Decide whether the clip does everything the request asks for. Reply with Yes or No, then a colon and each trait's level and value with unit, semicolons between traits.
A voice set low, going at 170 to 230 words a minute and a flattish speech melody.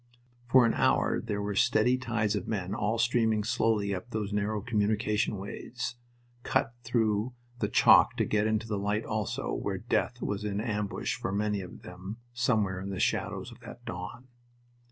Yes: low, 105 Hz; average, 175 wpm; narrow, 2.1 semitones